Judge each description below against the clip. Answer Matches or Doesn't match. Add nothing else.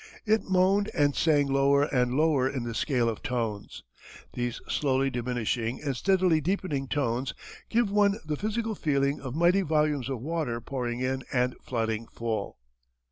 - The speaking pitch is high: Doesn't match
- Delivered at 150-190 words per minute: Matches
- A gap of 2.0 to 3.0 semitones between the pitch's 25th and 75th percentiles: Doesn't match